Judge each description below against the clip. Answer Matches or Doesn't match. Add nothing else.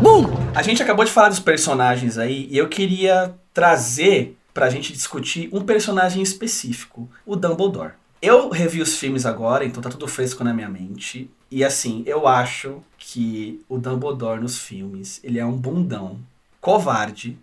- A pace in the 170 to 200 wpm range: Doesn't match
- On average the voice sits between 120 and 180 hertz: Matches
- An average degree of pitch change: Doesn't match